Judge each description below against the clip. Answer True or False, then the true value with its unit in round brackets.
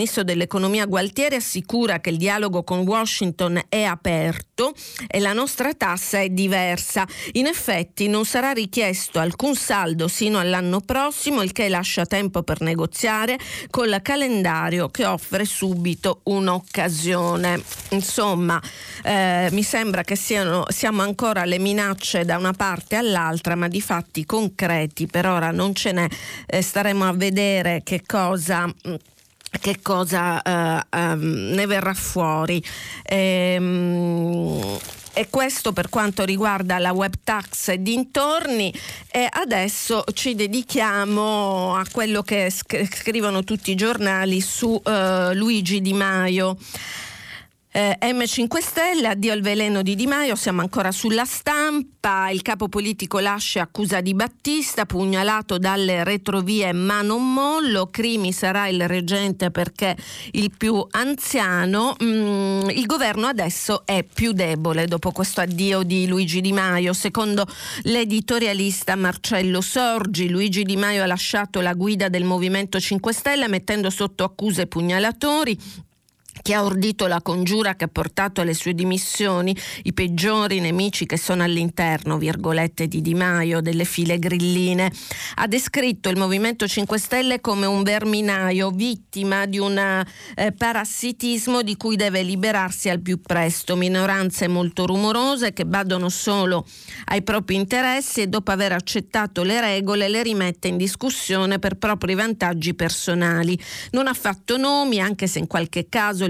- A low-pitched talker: False (195 Hz)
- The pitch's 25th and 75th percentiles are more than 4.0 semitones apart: False (3.1 semitones)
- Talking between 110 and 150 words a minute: True (140 wpm)